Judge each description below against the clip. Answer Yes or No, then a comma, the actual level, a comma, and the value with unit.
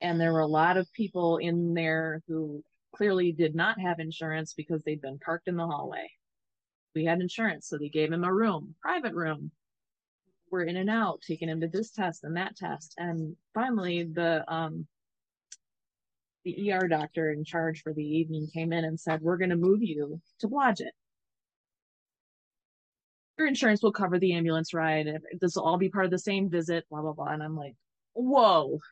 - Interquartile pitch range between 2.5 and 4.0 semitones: Yes, average, 2.8 semitones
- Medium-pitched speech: Yes, medium, 165 Hz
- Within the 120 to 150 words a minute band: No, average, 190 wpm